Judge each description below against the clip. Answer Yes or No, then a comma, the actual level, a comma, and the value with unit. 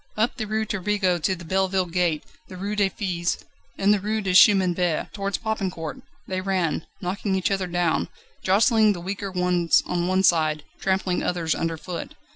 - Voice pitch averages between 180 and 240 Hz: Yes, medium, 185 Hz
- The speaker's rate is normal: Yes, average, 175 wpm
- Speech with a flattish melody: Yes, narrow, 2.3 semitones